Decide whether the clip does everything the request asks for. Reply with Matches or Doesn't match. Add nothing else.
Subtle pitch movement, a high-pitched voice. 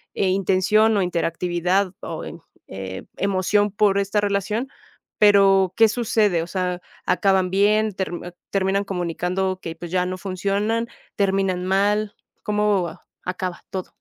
Matches